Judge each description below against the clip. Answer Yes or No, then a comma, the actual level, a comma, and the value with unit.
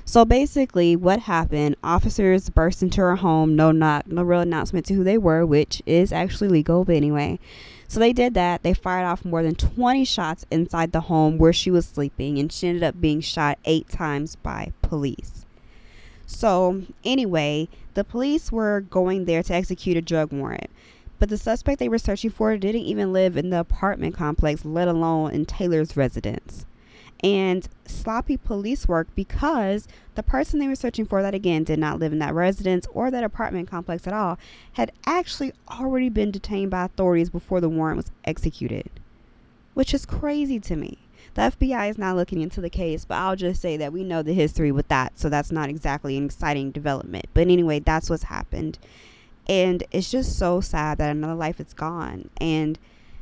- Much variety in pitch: No, average, 4.1 semitones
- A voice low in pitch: No, medium, 175 Hz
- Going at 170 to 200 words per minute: Yes, average, 190 wpm